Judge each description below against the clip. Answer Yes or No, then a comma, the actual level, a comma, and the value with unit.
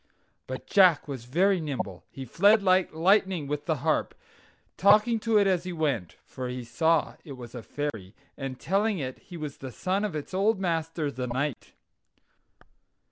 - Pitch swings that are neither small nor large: No, wide, 6.4 semitones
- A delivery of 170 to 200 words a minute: Yes, average, 175 wpm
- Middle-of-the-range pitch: Yes, medium, 160 Hz